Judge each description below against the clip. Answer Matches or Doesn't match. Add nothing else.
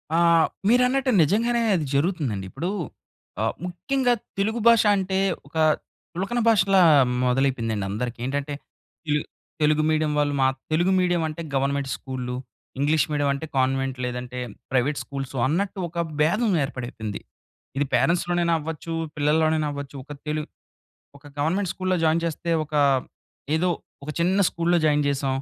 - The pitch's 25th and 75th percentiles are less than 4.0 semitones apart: Doesn't match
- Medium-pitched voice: Matches